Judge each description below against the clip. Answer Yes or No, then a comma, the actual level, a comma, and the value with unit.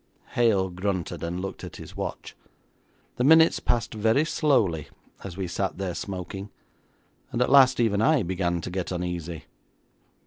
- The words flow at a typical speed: Yes, average, 150 wpm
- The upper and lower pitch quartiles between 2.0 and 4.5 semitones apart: No, average, 5.0 semitones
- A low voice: Yes, very low, 95 Hz